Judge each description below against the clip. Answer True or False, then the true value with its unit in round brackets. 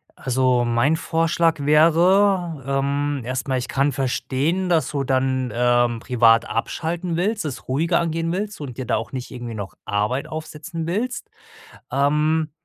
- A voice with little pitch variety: False (4.4 semitones)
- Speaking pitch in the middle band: True (145 Hz)